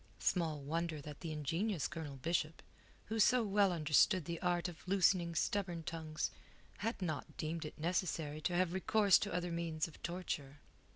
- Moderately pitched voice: Yes, medium, 170 Hz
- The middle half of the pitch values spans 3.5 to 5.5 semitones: No, average, 2.9 semitones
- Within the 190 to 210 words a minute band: No, average, 165 wpm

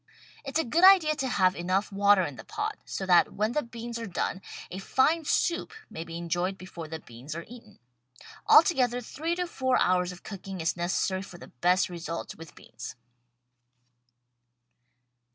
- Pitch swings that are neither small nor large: No, wide, 6.9 semitones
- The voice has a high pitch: Yes, high, 195 Hz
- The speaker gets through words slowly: No, average, 170 wpm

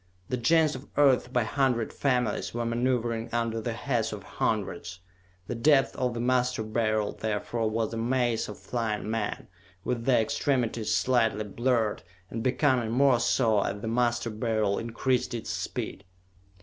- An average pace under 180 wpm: Yes, average, 155 wpm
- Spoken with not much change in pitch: Yes, narrow, 2.2 semitones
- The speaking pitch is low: Yes, low, 115 Hz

